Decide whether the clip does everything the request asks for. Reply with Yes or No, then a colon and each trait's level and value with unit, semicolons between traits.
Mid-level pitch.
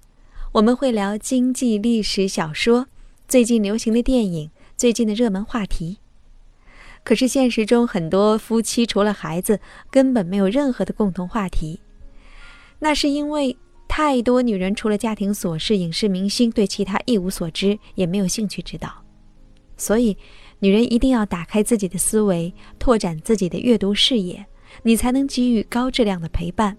No: high, 215 Hz